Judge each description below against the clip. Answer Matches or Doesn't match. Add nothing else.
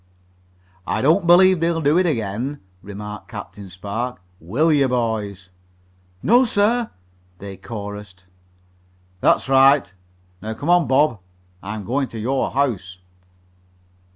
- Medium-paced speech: Doesn't match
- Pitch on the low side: Matches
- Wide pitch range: Matches